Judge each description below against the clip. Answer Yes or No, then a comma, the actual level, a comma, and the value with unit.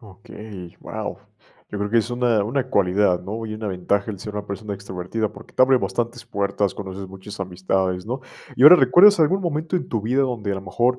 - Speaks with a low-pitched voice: Yes, low, 105 Hz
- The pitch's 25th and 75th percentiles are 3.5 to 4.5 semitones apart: Yes, average, 4.2 semitones